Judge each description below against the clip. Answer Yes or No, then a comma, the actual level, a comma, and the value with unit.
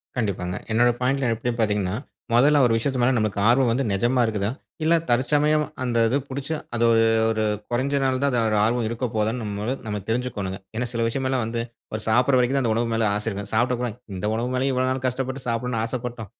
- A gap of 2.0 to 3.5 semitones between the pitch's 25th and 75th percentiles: Yes, average, 2.8 semitones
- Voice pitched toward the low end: Yes, low, 120 Hz